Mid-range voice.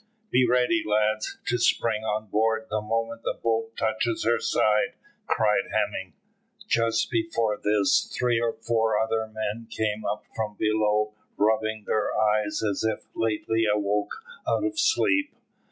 No: low, 110 Hz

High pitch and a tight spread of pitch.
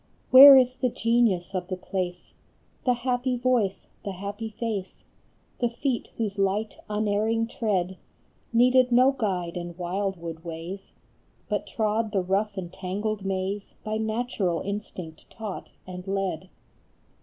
No: high, 205 Hz; average, 3.7 semitones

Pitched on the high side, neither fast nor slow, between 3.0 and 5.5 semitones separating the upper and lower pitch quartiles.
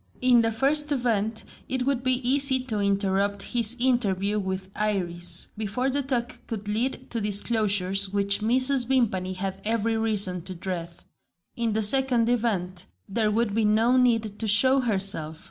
Yes: high, 220 Hz; average, 160 wpm; average, 3.8 semitones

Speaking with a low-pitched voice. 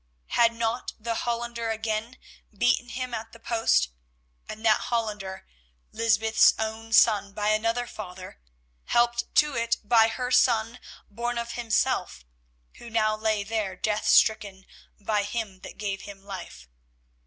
No: high, 220 Hz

